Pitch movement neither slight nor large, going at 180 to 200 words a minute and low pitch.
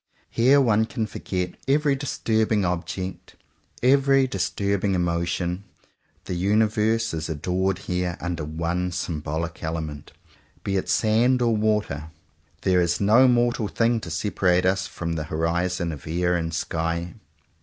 No: average, 4.5 semitones; average, 140 wpm; very low, 90 Hz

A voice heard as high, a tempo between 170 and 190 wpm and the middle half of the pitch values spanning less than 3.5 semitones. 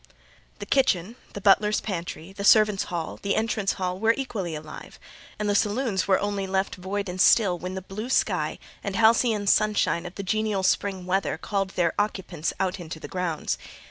Yes: high, 195 Hz; average, 180 wpm; narrow, 2.5 semitones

